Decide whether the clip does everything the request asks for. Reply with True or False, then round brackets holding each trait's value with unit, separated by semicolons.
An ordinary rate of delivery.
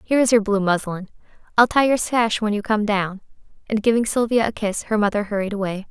False (215 wpm)